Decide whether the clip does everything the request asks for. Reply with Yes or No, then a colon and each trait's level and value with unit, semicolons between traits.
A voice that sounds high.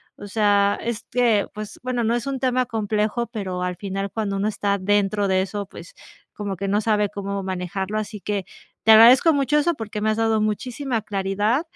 Yes: high, 210 Hz